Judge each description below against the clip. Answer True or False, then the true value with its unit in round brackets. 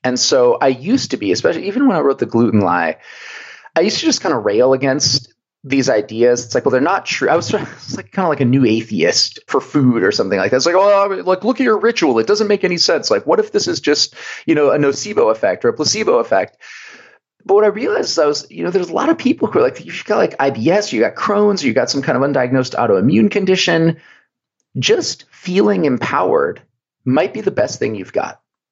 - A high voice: True (195 Hz)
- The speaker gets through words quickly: True (240 wpm)